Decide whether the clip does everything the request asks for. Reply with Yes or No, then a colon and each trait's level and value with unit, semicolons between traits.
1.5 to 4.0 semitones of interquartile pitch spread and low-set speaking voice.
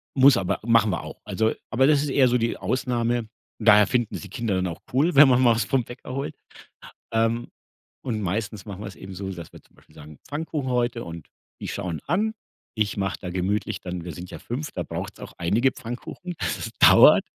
No: average, 5.0 semitones; low, 115 Hz